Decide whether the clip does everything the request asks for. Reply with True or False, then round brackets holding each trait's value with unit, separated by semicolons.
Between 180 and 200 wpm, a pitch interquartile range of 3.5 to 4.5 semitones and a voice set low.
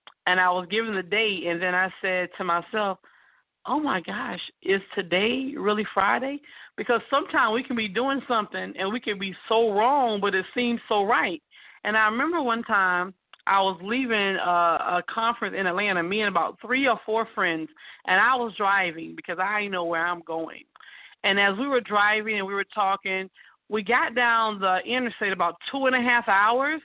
False (195 wpm; 4.1 semitones; 210 Hz)